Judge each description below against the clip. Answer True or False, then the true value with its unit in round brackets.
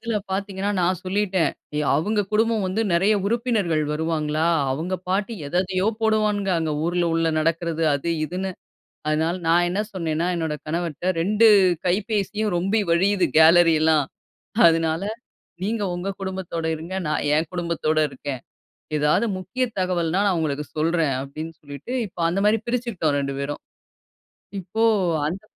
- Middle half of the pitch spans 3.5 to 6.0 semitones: True (3.9 semitones)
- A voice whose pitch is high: False (175 Hz)